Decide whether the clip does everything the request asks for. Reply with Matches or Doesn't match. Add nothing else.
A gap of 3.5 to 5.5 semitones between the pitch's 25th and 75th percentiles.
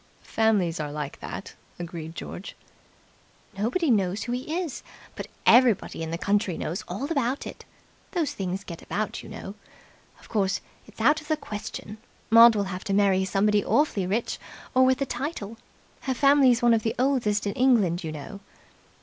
Matches